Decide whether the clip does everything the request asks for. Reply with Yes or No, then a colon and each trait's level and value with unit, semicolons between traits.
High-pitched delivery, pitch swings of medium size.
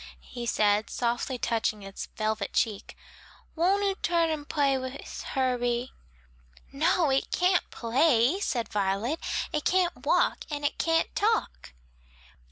No: very high, 265 Hz; wide, 6.0 semitones